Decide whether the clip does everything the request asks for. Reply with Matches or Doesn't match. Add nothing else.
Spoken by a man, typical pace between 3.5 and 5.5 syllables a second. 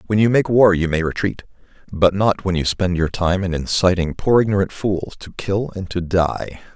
Matches